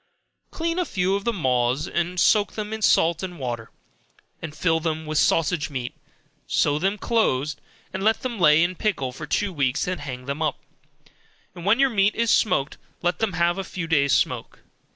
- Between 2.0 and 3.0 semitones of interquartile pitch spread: No, wide, 5.4 semitones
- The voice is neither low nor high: Yes, medium, 170 Hz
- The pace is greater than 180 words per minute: Yes, average, 190 wpm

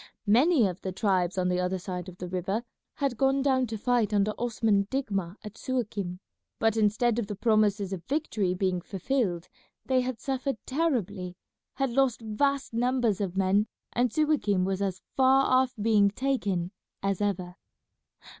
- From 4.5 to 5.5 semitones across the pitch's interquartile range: Yes, average, 5.2 semitones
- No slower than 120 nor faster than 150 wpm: No, average, 165 wpm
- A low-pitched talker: No, high, 210 Hz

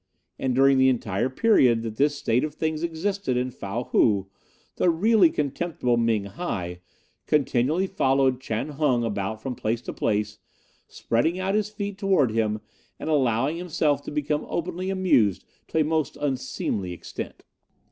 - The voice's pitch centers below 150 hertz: Yes, low, 135 Hz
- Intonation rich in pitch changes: Yes, wide, 6.0 semitones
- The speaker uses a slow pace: No, average, 155 wpm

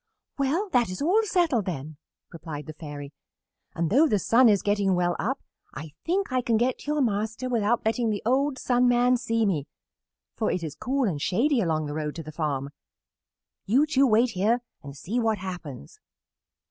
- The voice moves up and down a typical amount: No, wide, 7.4 semitones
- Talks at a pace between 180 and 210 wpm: Yes, average, 190 wpm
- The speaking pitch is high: Yes, high, 220 Hz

